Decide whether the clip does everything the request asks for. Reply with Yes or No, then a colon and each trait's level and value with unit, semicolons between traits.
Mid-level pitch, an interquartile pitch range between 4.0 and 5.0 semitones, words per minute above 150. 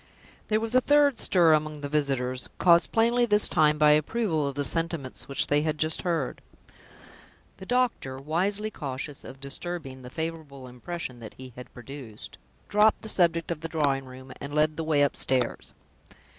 Yes: medium, 150 Hz; average, 4.4 semitones; average, 170 wpm